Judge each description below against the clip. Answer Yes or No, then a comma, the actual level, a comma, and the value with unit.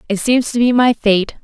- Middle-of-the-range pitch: No, high, 230 Hz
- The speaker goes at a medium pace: No, fast, 250 wpm